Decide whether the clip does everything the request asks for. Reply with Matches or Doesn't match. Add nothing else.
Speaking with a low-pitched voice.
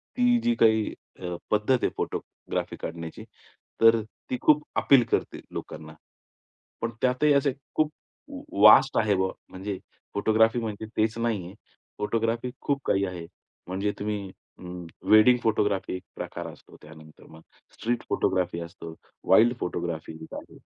Matches